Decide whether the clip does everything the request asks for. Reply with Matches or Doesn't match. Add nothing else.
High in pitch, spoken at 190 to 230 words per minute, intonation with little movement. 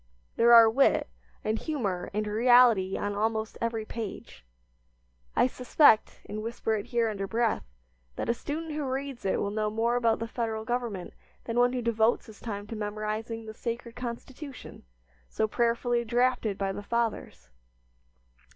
Doesn't match